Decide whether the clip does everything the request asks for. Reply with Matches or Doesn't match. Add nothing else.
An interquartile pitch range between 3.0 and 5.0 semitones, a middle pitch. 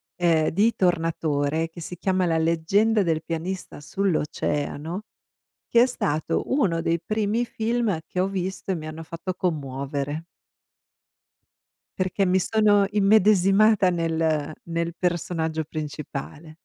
Matches